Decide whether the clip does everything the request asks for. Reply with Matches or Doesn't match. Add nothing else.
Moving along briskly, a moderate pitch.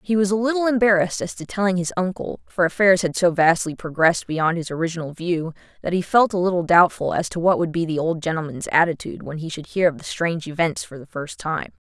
Matches